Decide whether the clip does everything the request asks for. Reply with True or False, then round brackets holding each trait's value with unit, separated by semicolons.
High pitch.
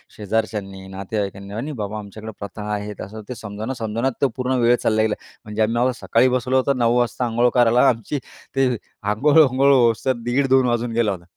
False (115 Hz)